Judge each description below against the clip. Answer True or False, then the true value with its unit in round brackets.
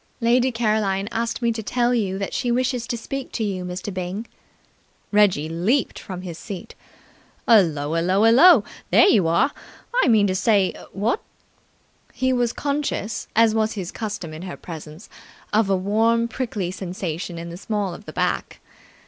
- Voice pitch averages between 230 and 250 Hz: False (210 Hz)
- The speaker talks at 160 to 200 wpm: True (165 wpm)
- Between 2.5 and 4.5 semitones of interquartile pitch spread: True (4.2 semitones)